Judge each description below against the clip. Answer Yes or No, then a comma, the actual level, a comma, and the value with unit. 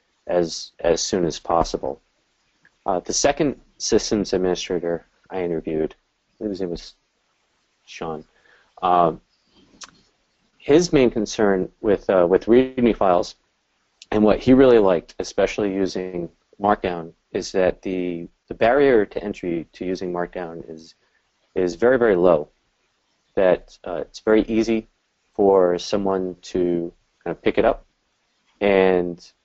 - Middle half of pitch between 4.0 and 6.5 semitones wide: No, average, 2.7 semitones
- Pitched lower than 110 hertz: Yes, very low, 90 Hz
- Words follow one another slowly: Yes, slow, 125 wpm